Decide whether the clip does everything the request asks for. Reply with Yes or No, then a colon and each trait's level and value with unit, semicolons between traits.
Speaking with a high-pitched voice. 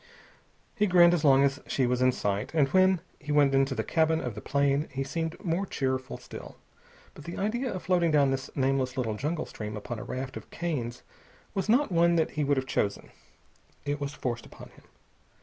No: medium, 140 Hz